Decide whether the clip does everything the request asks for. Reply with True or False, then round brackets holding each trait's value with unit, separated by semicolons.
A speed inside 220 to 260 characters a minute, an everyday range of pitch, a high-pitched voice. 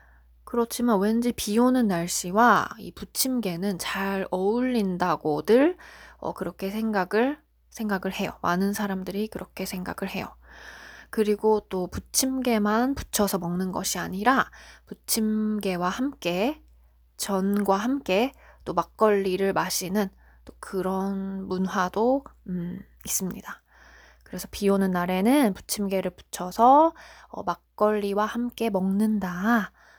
True (245 characters per minute; 3.3 semitones; 200 Hz)